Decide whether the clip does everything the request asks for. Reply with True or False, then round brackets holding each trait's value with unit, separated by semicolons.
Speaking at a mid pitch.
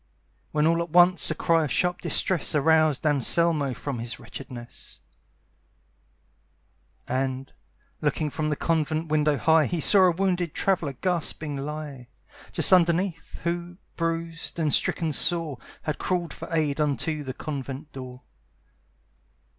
True (155 Hz)